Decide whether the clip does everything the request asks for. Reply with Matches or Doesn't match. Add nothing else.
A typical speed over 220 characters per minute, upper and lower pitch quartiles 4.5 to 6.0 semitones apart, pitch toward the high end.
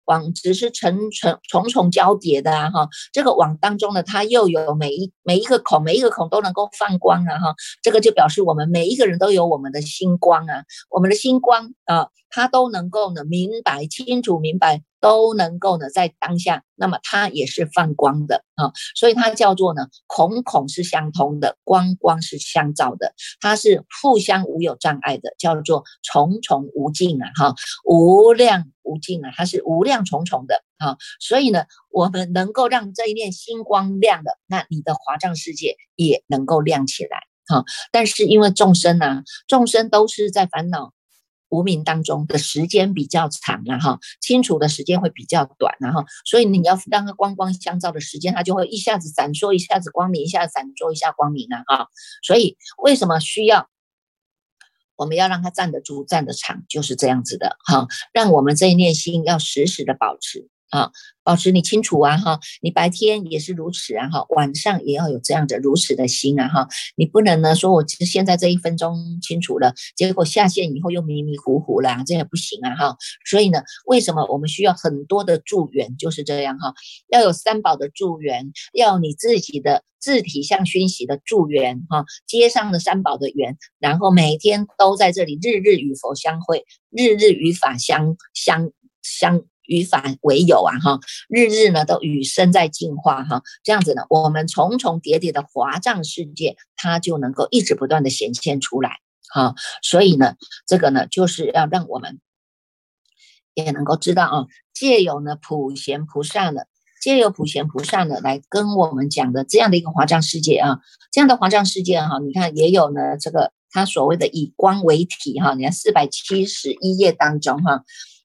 Doesn't match